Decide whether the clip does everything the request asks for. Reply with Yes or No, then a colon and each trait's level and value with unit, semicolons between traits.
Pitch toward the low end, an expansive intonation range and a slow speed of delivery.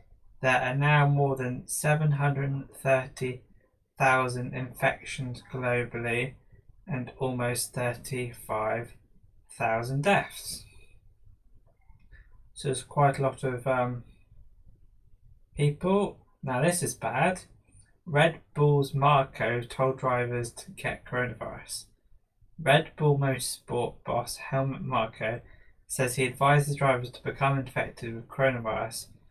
No: low, 125 Hz; average, 3.7 semitones; slow, 95 wpm